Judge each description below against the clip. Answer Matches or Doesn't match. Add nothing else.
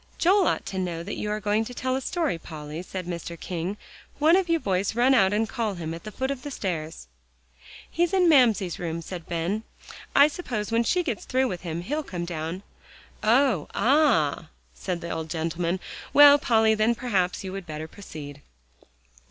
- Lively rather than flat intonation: Matches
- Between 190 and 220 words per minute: Matches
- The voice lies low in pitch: Doesn't match